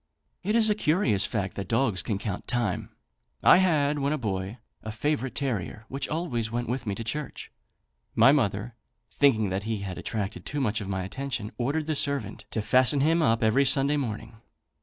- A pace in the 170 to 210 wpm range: Yes, average, 185 wpm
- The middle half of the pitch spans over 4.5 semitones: Yes, average, 5.2 semitones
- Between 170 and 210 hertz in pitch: No, low, 120 Hz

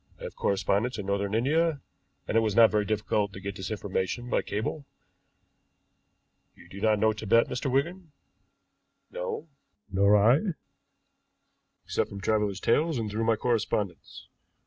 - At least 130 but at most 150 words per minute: Yes, average, 145 wpm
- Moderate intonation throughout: Yes, average, 3.6 semitones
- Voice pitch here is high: No, low, 110 Hz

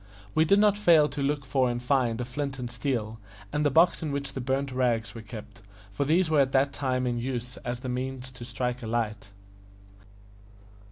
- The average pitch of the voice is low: Yes, low, 130 Hz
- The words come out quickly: Yes, fast, 210 wpm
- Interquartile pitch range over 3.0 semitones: No, average, 2.7 semitones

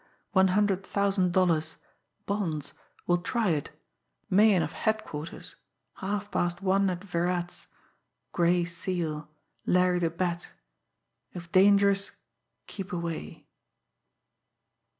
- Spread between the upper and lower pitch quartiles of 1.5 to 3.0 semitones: Yes, narrow, 2.5 semitones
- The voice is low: No, medium, 180 Hz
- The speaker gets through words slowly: Yes, slow, 100 wpm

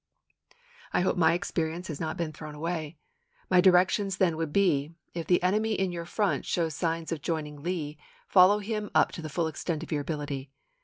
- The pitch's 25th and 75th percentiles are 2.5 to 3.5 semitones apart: Yes, average, 2.9 semitones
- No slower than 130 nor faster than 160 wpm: No, average, 195 wpm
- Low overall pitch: No, medium, 165 Hz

